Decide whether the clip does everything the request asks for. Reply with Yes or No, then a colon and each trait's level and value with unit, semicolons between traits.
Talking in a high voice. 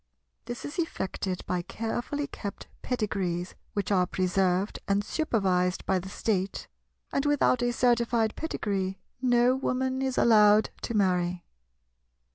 Yes: high, 210 Hz